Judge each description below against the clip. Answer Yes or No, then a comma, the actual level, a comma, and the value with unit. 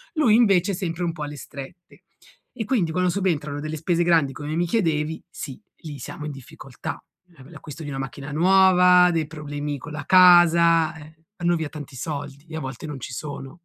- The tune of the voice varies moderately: Yes, average, 3.2 semitones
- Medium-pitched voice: Yes, medium, 160 Hz